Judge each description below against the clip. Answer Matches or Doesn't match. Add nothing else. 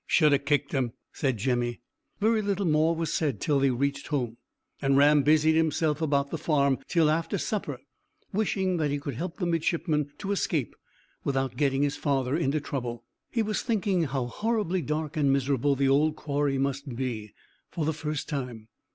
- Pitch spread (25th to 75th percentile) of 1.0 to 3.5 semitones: Matches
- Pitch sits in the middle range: Matches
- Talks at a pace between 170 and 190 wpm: Matches